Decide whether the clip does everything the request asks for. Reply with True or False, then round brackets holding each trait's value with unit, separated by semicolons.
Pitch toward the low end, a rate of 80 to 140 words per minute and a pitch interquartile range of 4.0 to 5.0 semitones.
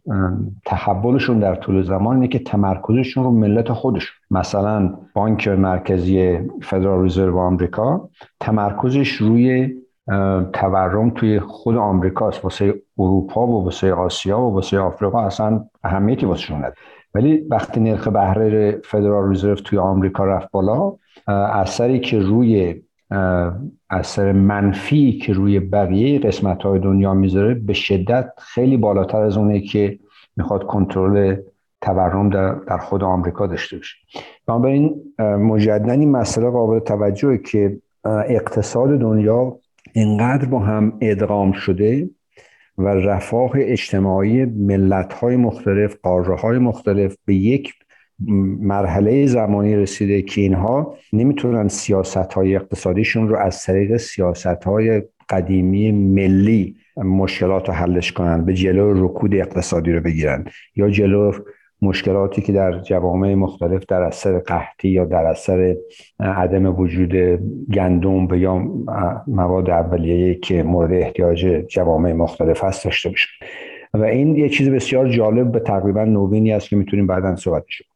False (100 Hz; 130 wpm; 2.7 semitones)